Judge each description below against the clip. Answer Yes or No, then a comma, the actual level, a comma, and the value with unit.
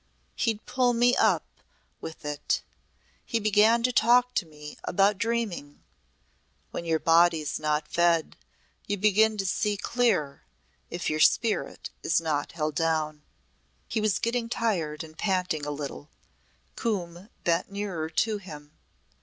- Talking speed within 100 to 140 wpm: Yes, slow, 135 wpm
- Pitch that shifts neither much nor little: No, wide, 5.9 semitones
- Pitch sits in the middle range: Yes, medium, 180 Hz